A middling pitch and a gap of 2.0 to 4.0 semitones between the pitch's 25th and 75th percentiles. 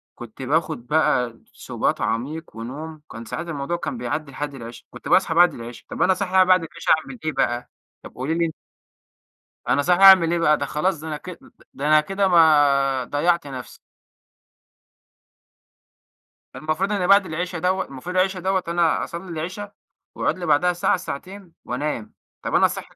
No: medium, 160 Hz; average, 4.6 semitones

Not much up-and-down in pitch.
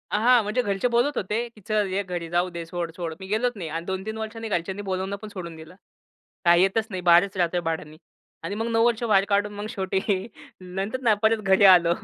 No: average, 3.6 semitones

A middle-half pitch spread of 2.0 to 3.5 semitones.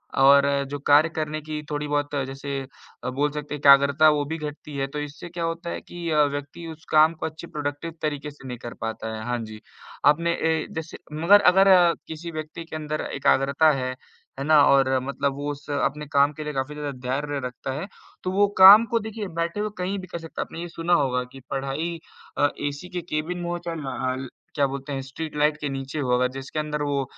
Yes: average, 2.8 semitones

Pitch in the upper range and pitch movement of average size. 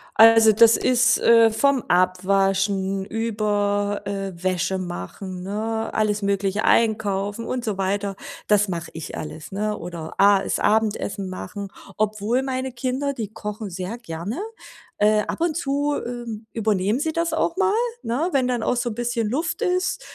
Yes: high, 215 Hz; average, 3.6 semitones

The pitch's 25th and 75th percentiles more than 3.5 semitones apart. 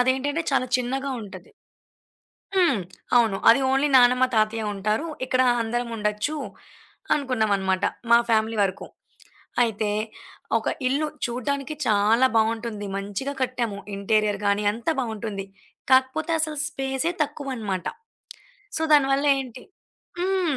Yes: average, 4.1 semitones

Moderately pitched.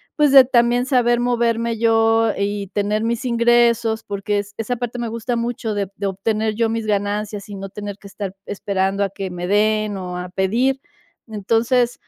No: high, 220 Hz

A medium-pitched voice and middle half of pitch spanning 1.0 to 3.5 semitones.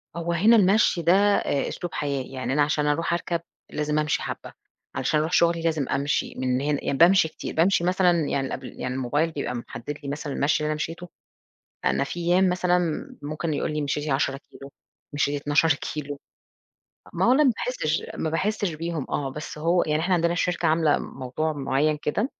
Yes: medium, 155 Hz; average, 3.1 semitones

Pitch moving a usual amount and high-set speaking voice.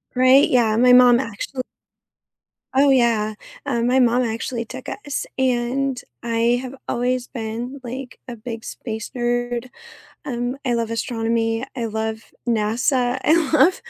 No: narrow, 1.9 semitones; high, 245 Hz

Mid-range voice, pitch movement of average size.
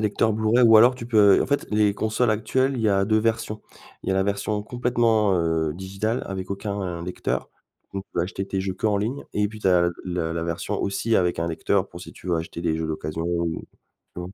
No: low, 100 Hz; average, 3.7 semitones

